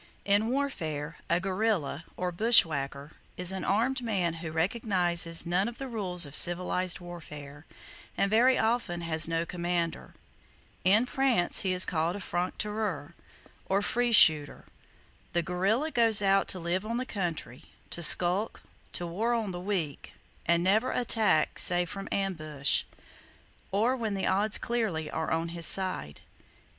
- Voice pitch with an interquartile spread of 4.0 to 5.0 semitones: Yes, average, 4.4 semitones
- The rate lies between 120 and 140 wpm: No, average, 150 wpm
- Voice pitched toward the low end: No, medium, 180 Hz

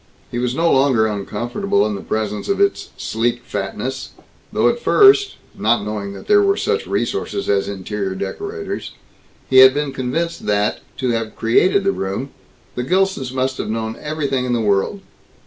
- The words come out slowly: No, average, 170 wpm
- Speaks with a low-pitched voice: Yes, low, 125 Hz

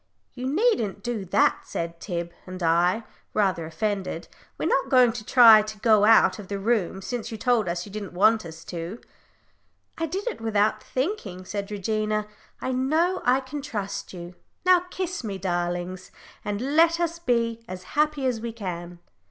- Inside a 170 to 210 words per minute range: Yes, average, 175 wpm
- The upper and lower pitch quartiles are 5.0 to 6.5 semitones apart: Yes, wide, 5.6 semitones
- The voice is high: Yes, high, 215 Hz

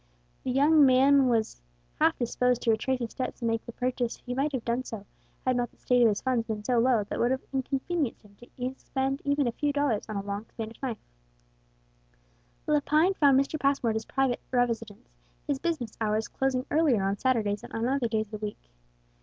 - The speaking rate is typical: No, fast, 210 wpm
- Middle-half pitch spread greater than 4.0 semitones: No, average, 3.1 semitones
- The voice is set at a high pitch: Yes, very high, 250 Hz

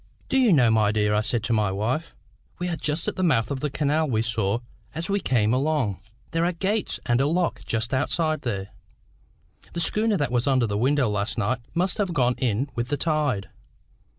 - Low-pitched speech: Yes, low, 130 Hz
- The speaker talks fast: Yes, fast, 210 wpm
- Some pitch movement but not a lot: No, wide, 6.5 semitones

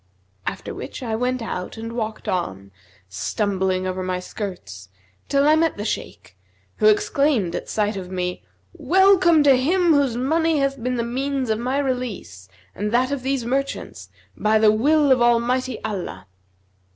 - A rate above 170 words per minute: No, average, 165 wpm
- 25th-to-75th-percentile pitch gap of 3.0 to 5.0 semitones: No, wide, 5.5 semitones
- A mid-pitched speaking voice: No, high, 240 Hz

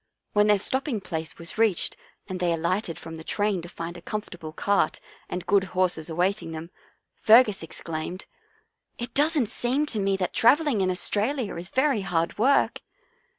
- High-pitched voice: Yes, high, 195 Hz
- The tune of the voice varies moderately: Yes, average, 4.9 semitones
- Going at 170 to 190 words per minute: Yes, average, 175 wpm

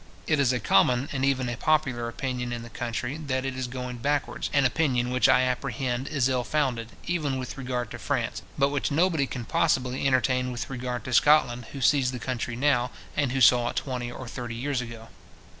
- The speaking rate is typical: No, fast, 210 wpm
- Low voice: Yes, low, 130 Hz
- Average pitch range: No, narrow, 2.1 semitones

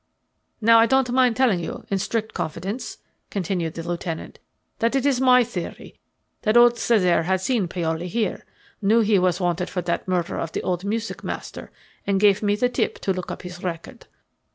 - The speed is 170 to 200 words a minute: Yes, average, 185 wpm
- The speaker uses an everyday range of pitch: Yes, average, 4.6 semitones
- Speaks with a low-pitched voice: No, high, 195 Hz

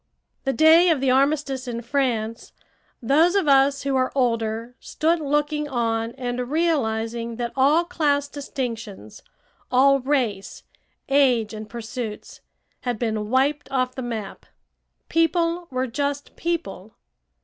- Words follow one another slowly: Yes, slow, 125 wpm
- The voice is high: Yes, very high, 260 Hz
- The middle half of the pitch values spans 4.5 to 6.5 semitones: No, average, 4.0 semitones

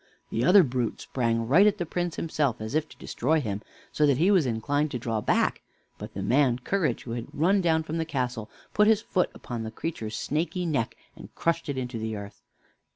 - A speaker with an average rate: No, fast, 220 wpm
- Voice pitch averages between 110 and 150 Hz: Yes, medium, 140 Hz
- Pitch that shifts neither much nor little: No, wide, 6.2 semitones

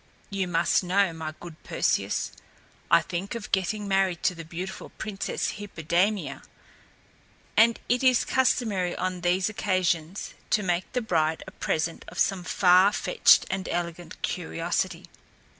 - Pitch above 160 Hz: Yes, medium, 185 Hz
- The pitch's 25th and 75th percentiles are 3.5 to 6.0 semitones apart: No, average, 2.8 semitones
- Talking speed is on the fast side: No, average, 140 wpm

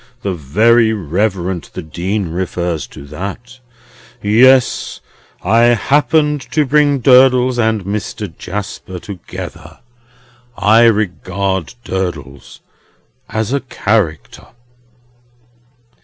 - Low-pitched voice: Yes, low, 105 Hz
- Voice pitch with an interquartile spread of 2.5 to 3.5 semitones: No, average, 5.2 semitones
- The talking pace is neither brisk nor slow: No, slow, 90 wpm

